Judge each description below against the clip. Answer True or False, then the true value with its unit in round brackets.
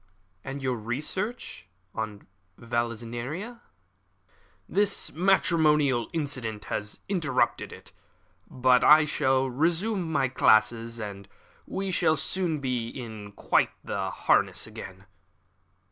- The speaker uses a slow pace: True (100 wpm)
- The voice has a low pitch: True (130 Hz)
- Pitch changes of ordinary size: False (5.9 semitones)